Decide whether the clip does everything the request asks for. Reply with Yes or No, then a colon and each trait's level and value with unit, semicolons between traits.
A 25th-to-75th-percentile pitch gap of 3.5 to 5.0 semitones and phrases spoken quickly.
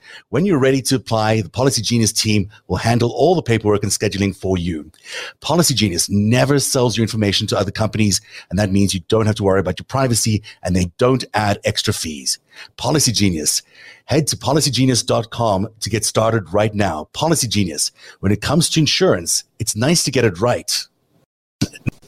No: average, 4.1 semitones; average, 180 wpm